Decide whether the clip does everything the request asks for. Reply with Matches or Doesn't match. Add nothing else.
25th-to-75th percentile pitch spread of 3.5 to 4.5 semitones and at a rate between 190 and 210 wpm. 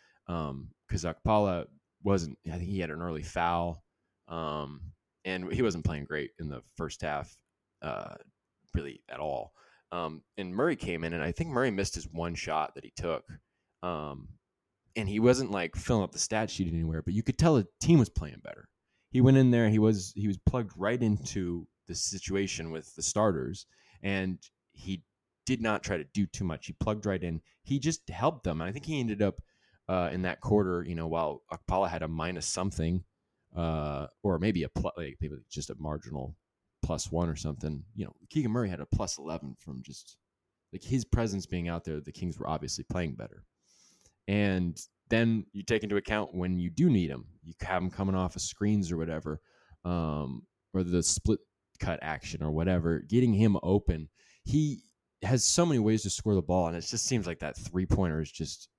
Matches